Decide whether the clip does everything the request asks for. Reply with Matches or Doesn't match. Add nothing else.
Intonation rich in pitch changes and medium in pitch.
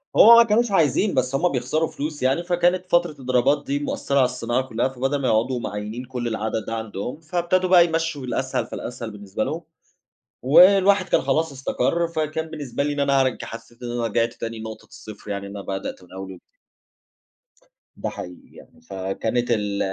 Doesn't match